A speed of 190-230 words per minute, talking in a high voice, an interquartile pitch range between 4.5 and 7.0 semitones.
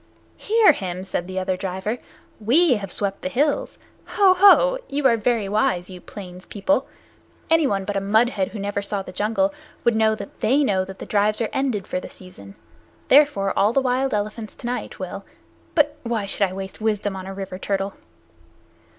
Yes: average, 195 wpm; high, 210 Hz; average, 4.9 semitones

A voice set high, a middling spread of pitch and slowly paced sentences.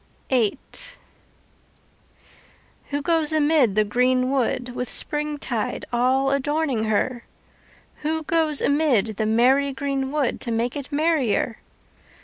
Yes: very high, 270 Hz; average, 3.6 semitones; slow, 115 wpm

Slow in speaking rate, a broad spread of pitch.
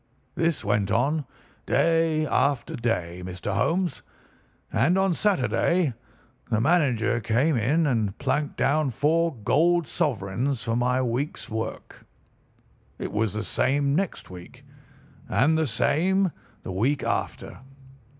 Yes: slow, 120 wpm; wide, 6.2 semitones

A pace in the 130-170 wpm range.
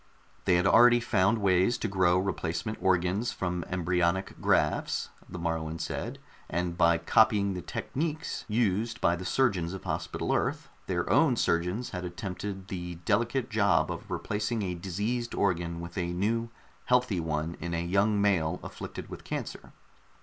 Yes: average, 155 wpm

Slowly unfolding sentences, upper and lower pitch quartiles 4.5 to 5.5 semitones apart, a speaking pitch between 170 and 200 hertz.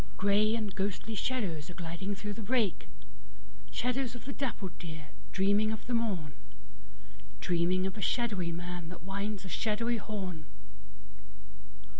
Yes: slow, 130 wpm; average, 5.2 semitones; high, 190 Hz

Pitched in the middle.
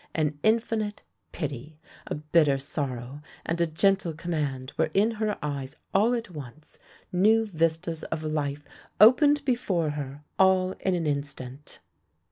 Yes: medium, 160 Hz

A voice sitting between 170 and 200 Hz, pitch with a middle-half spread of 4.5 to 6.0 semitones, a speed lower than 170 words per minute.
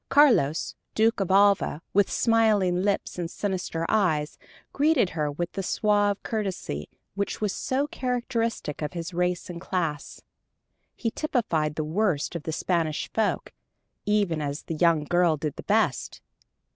Yes: medium, 185 Hz; average, 4.9 semitones; average, 145 wpm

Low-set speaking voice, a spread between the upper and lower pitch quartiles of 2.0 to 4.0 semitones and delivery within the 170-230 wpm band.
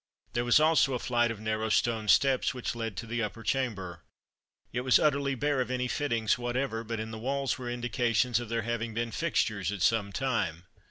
Yes: low, 120 Hz; narrow, 2.5 semitones; fast, 205 wpm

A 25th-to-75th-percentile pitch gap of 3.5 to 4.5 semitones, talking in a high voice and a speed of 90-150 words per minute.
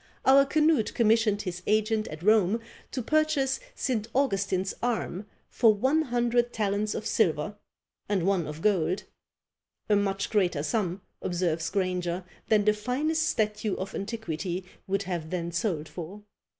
Yes: average, 4.2 semitones; high, 205 Hz; average, 140 wpm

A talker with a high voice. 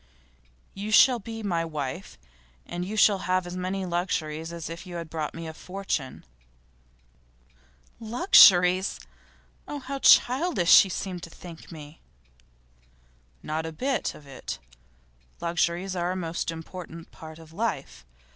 No: medium, 175 Hz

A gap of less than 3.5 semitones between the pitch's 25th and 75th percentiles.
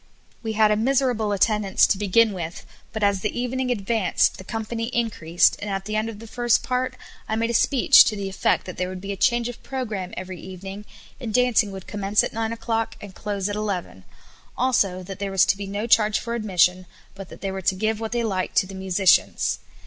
Yes: average, 3.0 semitones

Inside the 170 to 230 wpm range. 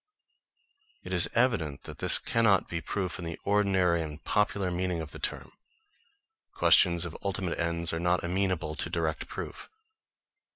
No: average, 155 wpm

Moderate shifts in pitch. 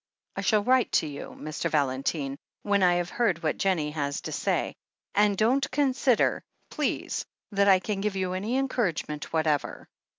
No: wide, 5.8 semitones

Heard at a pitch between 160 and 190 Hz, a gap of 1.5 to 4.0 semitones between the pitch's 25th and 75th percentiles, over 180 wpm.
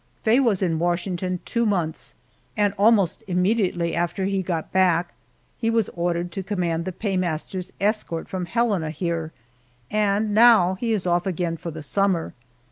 No: medium, 185 Hz; average, 3.1 semitones; average, 155 wpm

